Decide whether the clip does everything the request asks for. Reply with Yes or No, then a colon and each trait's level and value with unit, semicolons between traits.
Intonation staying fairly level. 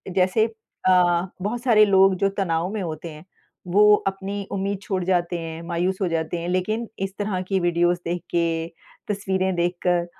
Yes: narrow, 2.3 semitones